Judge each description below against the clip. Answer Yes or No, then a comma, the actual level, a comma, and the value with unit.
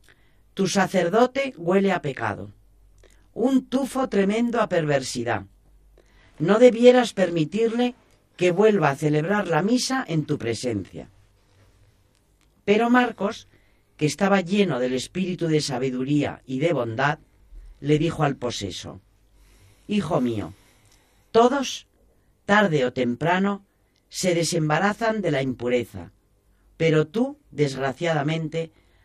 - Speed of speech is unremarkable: No, slow, 105 wpm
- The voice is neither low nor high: Yes, medium, 150 Hz